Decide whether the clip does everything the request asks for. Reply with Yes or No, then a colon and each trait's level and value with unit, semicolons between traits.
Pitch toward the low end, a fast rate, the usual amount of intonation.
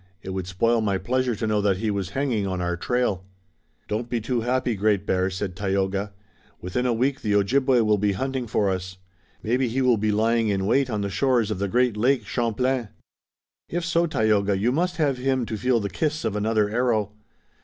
Yes: low, 110 Hz; fast, 210 wpm; average, 4.0 semitones